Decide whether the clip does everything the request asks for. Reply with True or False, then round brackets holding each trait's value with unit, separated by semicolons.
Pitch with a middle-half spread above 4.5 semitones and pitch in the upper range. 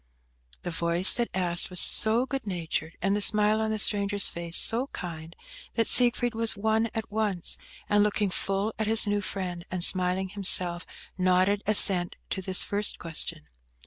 False (3.4 semitones; 200 Hz)